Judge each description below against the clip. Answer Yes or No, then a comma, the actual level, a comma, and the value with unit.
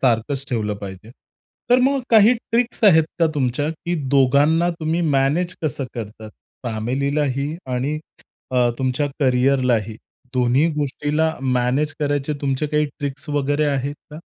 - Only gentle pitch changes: No, average, 3.3 semitones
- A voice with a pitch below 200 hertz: Yes, medium, 140 Hz